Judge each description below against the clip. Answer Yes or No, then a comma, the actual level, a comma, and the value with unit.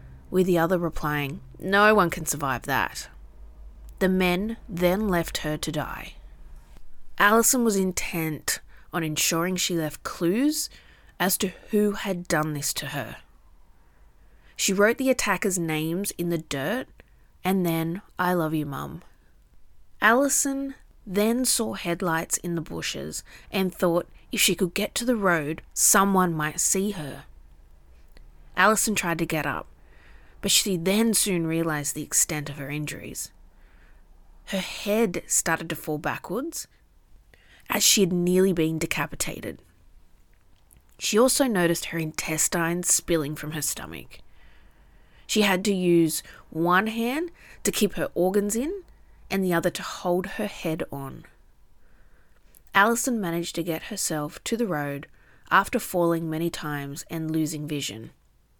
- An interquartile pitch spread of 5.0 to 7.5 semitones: Yes, wide, 5.6 semitones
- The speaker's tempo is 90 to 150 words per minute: Yes, average, 140 wpm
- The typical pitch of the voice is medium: Yes, medium, 165 Hz